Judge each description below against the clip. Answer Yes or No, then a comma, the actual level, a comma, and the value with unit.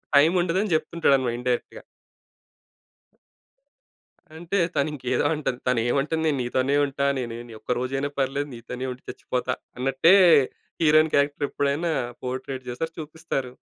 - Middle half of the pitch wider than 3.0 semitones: Yes, average, 3.5 semitones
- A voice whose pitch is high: No, medium, 140 Hz